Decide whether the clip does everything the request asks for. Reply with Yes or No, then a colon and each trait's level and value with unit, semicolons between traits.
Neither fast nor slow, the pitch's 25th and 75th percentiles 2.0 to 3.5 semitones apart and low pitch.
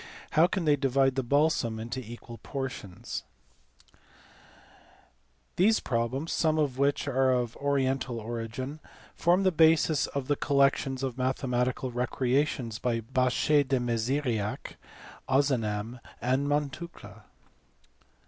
No: slow, 110 wpm; average, 3.1 semitones; low, 130 Hz